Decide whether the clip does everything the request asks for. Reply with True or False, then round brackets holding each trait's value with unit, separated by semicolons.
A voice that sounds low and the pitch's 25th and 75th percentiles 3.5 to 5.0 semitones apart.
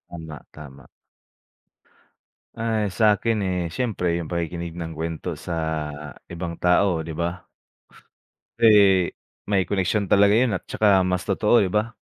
True (90 Hz; 3.9 semitones)